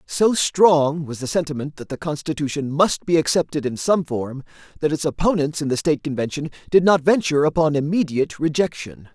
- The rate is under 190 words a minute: Yes, average, 175 wpm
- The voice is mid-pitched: Yes, medium, 155 Hz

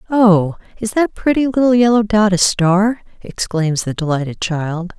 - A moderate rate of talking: Yes, average, 155 wpm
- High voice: Yes, high, 200 Hz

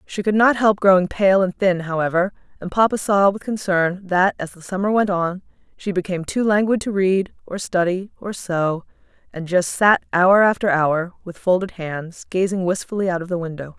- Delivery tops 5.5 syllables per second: No, 5.0 syllables/s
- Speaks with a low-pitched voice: No, medium, 185 Hz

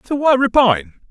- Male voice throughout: Yes, male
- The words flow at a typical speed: Yes, average, 165 wpm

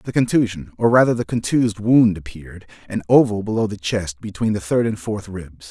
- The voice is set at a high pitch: No, low, 105 Hz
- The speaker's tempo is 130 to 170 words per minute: No, average, 190 wpm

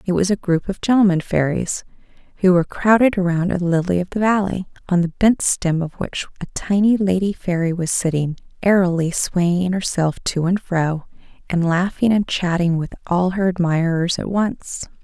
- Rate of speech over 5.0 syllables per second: No, 4.8 syllables/s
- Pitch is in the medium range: Yes, medium, 180 Hz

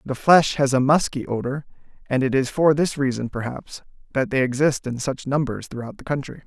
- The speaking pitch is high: No, low, 135 Hz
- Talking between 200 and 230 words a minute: Yes, fast, 205 wpm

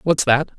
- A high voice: No, medium, 145 Hz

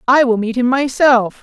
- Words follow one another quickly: Yes, fast, 210 wpm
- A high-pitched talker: Yes, very high, 250 Hz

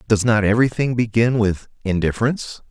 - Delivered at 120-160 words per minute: Yes, slow, 135 wpm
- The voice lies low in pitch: Yes, low, 115 Hz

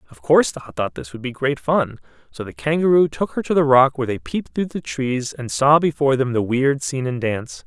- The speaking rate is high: Yes, fast, 250 wpm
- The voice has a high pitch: No, low, 135 Hz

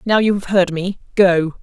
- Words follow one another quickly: Yes, fast, 220 wpm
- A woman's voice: Yes, female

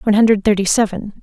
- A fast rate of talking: No, average, 195 wpm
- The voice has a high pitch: Yes, high, 210 Hz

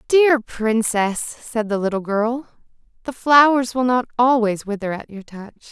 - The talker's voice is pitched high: Yes, high, 235 Hz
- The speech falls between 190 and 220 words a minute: No, average, 160 wpm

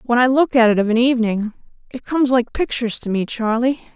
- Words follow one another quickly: Yes, fast, 225 wpm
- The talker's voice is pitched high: Yes, high, 240 Hz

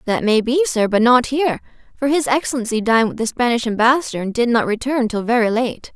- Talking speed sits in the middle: No, fast, 220 wpm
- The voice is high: Yes, high, 235 Hz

